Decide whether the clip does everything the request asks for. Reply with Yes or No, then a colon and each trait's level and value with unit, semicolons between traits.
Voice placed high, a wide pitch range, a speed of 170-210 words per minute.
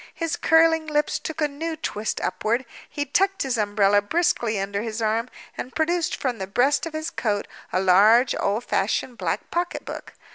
Yes: very high, 250 Hz; wide, 7.0 semitones; average, 175 wpm